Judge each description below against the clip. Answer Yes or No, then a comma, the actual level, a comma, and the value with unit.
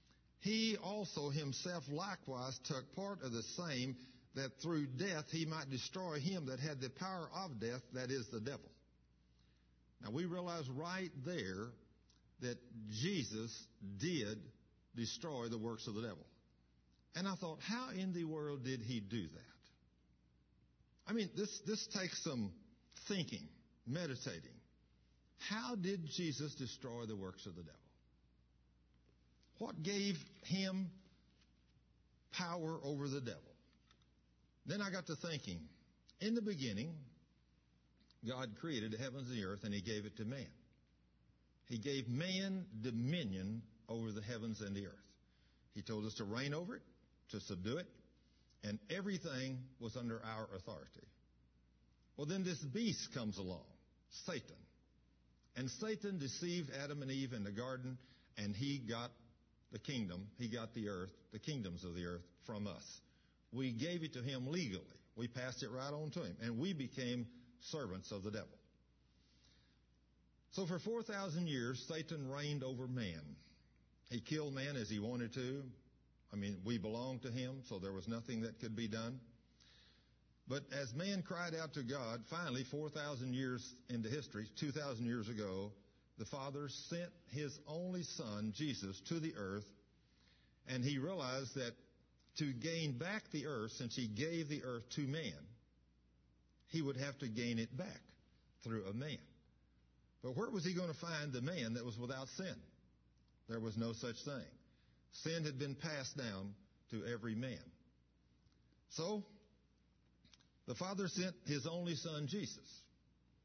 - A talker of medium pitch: No, low, 120 Hz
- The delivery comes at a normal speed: Yes, average, 150 wpm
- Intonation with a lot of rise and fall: Yes, wide, 9.0 semitones